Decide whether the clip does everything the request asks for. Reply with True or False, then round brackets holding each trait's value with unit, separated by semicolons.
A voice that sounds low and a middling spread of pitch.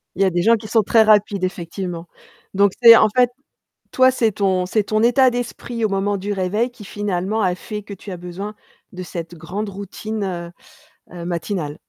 False (200 Hz; 3.1 semitones)